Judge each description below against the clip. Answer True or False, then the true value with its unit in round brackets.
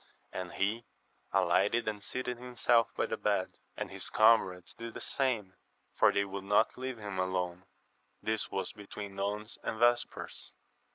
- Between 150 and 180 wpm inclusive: True (155 wpm)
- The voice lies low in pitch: True (105 Hz)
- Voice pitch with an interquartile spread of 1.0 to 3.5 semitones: True (3.1 semitones)